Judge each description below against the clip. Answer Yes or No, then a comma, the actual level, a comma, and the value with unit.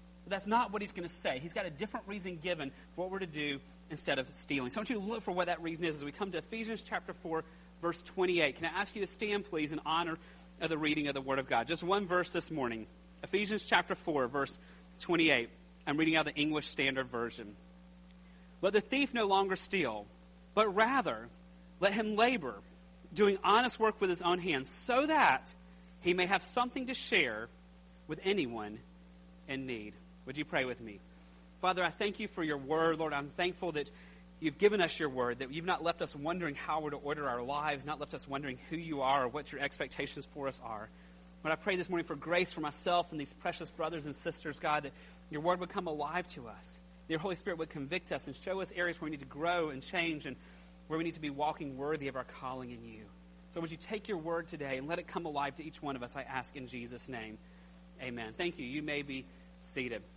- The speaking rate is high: Yes, fast, 235 wpm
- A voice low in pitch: No, medium, 150 Hz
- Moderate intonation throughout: No, wide, 6.5 semitones